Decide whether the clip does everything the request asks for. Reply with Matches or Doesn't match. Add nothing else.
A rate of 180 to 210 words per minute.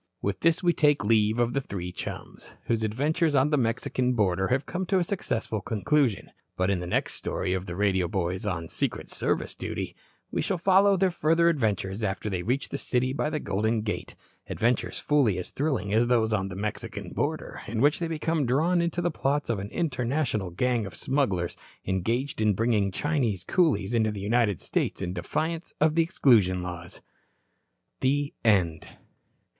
Matches